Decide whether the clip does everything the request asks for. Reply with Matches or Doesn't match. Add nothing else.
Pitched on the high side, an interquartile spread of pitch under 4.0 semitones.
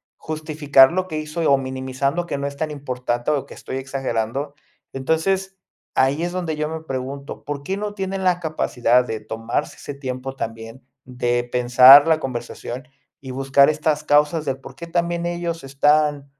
Doesn't match